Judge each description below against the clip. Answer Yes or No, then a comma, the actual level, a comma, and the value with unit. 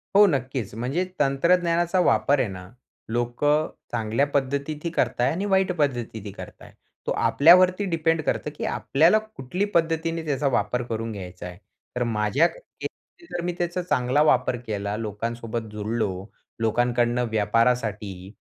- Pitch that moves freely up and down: Yes, wide, 6.6 semitones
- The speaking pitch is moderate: No, low, 125 Hz